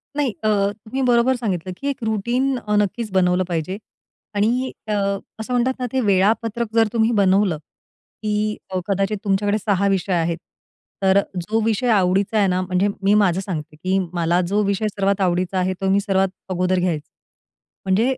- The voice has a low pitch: No, high, 200 Hz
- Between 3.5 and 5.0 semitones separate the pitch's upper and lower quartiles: No, average, 3.0 semitones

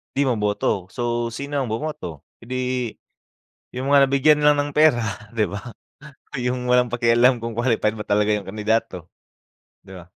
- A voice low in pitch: Yes, low, 120 Hz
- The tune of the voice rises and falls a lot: No, average, 3.9 semitones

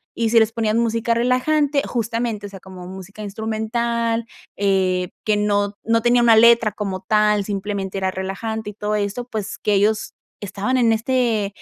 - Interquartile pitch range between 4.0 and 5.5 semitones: No, narrow, 2.5 semitones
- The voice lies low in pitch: No, high, 215 Hz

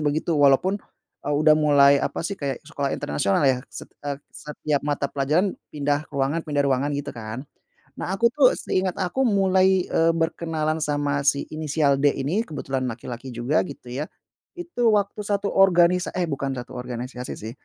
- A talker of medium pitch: Yes, medium, 150 Hz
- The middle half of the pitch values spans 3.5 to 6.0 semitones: Yes, average, 4.2 semitones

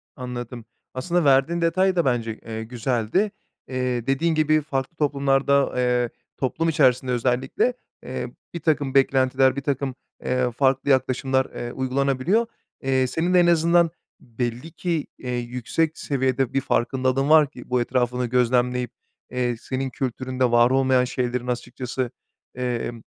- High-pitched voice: No, low, 130 Hz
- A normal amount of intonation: No, narrow, 2.2 semitones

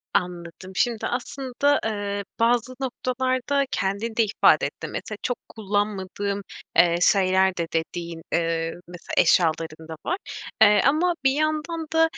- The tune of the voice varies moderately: No, wide, 6.4 semitones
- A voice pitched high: Yes, high, 205 Hz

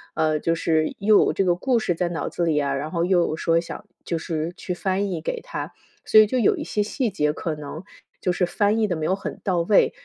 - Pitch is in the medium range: Yes, medium, 175 Hz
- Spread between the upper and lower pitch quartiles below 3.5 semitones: No, average, 3.8 semitones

